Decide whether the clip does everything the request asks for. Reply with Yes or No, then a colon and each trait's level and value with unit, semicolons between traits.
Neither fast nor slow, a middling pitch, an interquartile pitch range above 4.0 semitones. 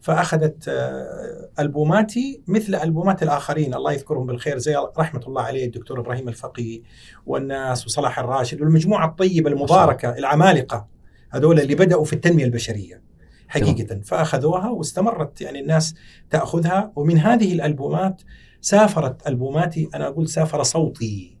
Yes: average, 120 wpm; medium, 150 Hz; average, 5.0 semitones